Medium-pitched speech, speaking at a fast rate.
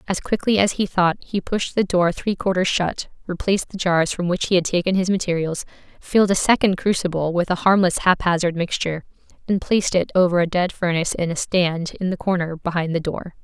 Yes: medium, 180 Hz; fast, 210 wpm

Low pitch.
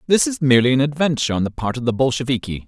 Yes: low, 130 Hz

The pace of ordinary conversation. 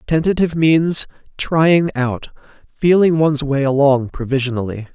No: slow, 110 wpm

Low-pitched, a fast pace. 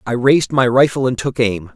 Yes: low, 125 Hz; fast, 240 wpm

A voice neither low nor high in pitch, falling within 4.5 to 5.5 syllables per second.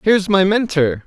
Yes: medium, 180 Hz; 5.2 syllables/s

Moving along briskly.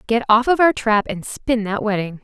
Yes: fast, 240 wpm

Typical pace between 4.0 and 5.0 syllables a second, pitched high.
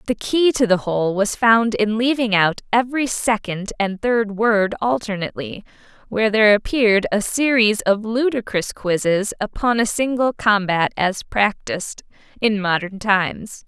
Yes: 4.6 syllables/s; high, 215 Hz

